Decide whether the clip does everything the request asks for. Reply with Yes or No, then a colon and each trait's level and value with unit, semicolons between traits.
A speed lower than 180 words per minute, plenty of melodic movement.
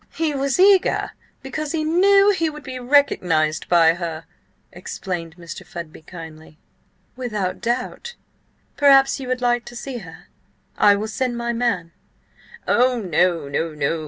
Yes: average, 140 wpm; wide, 8.3 semitones